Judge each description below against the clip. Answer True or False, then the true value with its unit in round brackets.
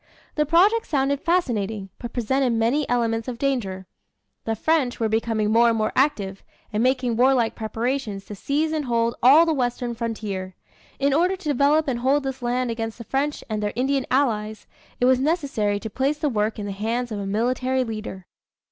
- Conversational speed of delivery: True (190 wpm)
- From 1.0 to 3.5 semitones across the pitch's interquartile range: False (4.0 semitones)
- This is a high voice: True (245 Hz)